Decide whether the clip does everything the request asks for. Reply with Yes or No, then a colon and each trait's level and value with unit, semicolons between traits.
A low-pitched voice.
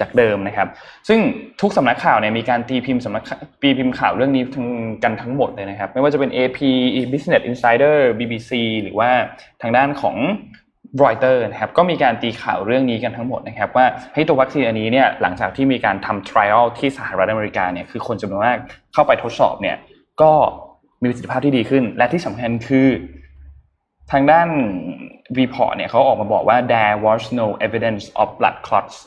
Yes: low, 125 Hz